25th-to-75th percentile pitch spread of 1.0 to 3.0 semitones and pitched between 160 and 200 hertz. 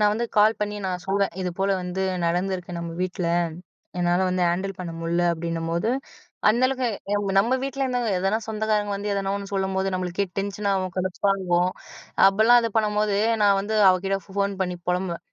Yes: narrow, 2.6 semitones; high, 195 Hz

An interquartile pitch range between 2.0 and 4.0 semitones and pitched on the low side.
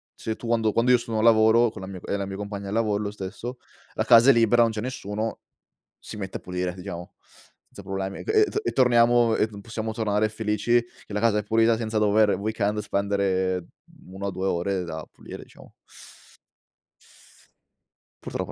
Yes: average, 2.7 semitones; low, 105 Hz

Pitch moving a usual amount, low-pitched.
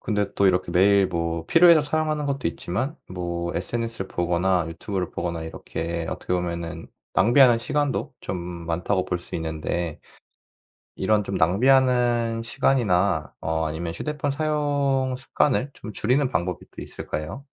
No: wide, 7.3 semitones; very low, 95 Hz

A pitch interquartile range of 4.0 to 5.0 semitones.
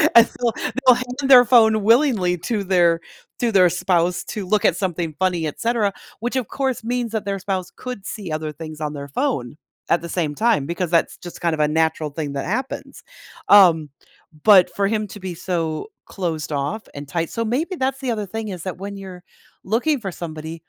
No: wide, 5.6 semitones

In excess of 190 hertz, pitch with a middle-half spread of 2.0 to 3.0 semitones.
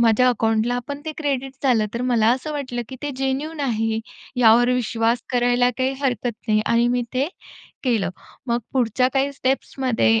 Yes: high, 245 Hz; narrow, 2.6 semitones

